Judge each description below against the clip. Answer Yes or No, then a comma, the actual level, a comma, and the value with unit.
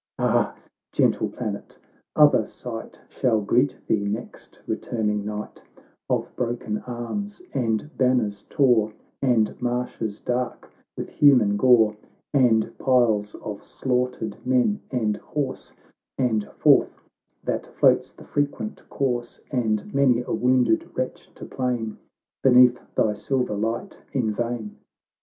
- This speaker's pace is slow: Yes, slow, 120 wpm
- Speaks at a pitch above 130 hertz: No, low, 120 Hz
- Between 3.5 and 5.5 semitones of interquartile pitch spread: No, average, 2.9 semitones